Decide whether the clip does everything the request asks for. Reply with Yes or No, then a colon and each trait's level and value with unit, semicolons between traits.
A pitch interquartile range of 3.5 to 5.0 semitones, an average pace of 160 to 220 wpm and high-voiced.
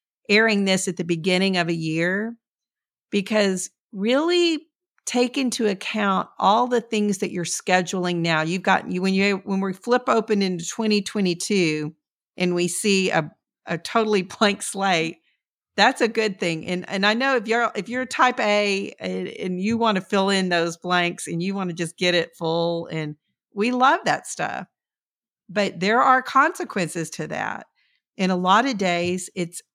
Yes: average, 4.0 semitones; average, 175 wpm; high, 195 Hz